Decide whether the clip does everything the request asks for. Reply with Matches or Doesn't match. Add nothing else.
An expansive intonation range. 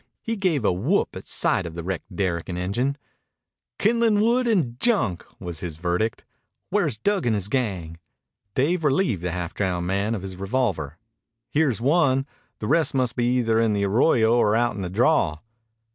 Matches